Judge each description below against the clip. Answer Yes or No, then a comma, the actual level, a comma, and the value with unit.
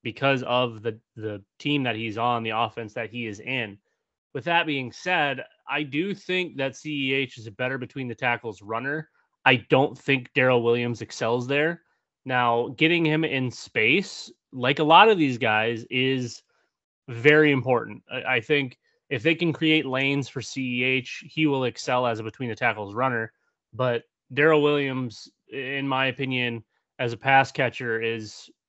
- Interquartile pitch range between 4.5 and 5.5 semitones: No, average, 3.3 semitones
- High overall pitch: No, low, 130 Hz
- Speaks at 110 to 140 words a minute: No, average, 165 wpm